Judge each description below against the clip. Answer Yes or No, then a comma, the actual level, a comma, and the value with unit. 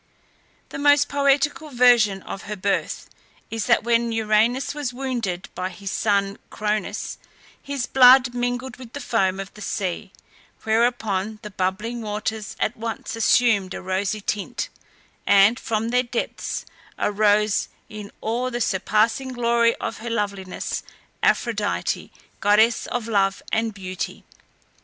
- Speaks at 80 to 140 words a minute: Yes, slow, 135 wpm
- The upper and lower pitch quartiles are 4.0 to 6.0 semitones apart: No, average, 3.2 semitones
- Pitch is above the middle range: Yes, high, 220 Hz